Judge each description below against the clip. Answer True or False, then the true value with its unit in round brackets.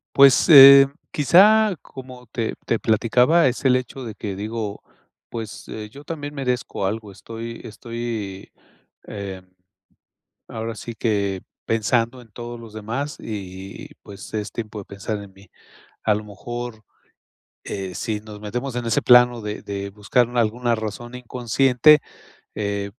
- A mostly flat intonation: False (3.1 semitones)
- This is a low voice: True (115 Hz)